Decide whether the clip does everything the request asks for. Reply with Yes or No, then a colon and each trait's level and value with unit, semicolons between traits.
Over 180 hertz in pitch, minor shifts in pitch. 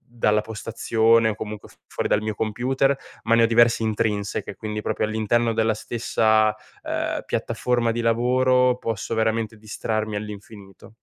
No: low, 110 Hz; narrow, 1.5 semitones